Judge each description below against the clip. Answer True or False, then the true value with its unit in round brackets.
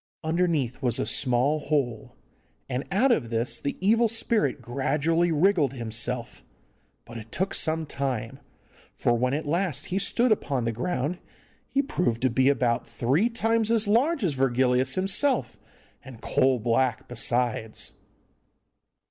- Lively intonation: True (7.3 semitones)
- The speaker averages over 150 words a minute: False (140 wpm)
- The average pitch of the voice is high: False (140 Hz)